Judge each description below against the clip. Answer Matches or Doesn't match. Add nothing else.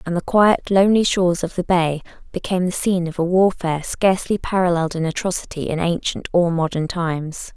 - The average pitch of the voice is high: Doesn't match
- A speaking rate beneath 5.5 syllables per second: Doesn't match